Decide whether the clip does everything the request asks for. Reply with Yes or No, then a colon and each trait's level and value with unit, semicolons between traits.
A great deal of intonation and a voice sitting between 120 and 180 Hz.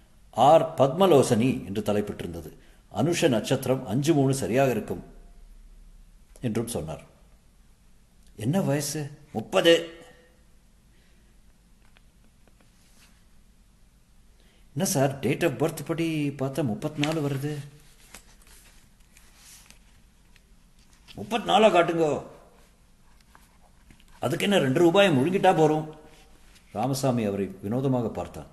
Yes: wide, 6.9 semitones; medium, 140 Hz